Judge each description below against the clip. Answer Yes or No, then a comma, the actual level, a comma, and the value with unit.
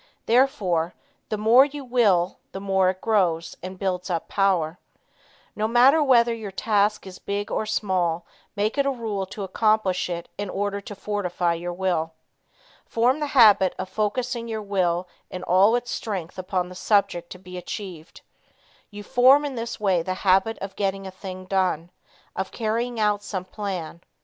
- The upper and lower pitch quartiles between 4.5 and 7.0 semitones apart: No, average, 3.3 semitones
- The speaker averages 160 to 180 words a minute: Yes, average, 170 wpm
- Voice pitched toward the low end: No, high, 200 Hz